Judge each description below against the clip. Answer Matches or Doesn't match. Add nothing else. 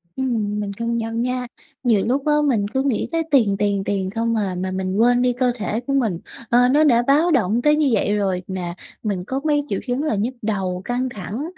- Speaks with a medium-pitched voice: Doesn't match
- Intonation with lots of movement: Doesn't match